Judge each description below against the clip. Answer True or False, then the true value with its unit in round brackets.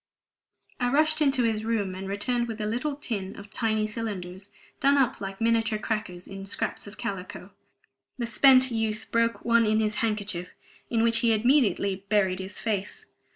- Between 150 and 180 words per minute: True (170 wpm)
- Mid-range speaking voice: False (220 Hz)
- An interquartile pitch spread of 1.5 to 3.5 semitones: True (2.8 semitones)